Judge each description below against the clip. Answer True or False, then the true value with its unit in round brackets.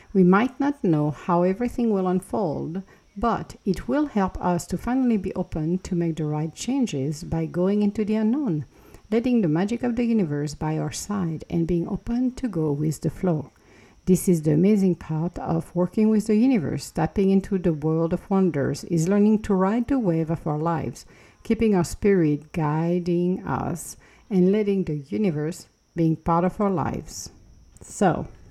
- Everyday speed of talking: True (175 wpm)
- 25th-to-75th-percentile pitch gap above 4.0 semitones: True (4.6 semitones)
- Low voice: False (180 Hz)